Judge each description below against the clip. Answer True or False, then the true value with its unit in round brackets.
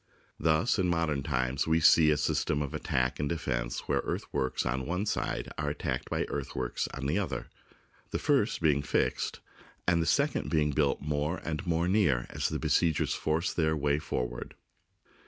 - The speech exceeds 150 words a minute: True (175 wpm)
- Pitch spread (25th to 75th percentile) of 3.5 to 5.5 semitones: False (3.1 semitones)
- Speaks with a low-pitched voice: True (75 Hz)